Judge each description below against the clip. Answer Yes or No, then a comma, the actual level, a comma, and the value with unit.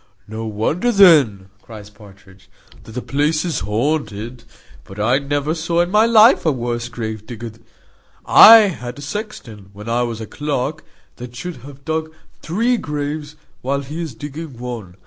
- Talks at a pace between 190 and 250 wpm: No, average, 160 wpm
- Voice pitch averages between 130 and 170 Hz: Yes, low, 135 Hz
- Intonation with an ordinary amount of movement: No, wide, 6.0 semitones